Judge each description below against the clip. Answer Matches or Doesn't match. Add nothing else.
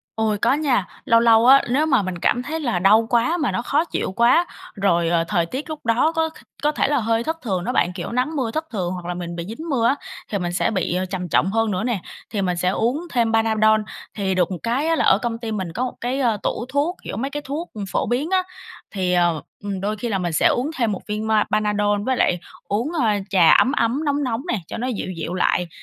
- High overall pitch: Matches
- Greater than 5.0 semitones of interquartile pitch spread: Matches